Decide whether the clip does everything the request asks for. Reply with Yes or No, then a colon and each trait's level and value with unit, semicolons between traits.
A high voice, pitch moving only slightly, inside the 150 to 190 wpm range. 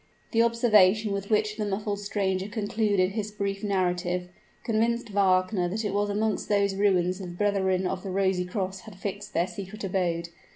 Yes: high, 200 Hz; narrow, 2.2 semitones; average, 170 wpm